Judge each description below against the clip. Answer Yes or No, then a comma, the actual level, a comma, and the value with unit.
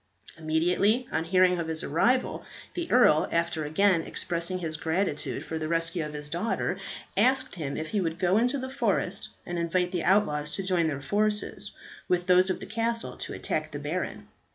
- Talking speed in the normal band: Yes, average, 185 wpm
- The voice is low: No, medium, 180 Hz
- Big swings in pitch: No, average, 4.1 semitones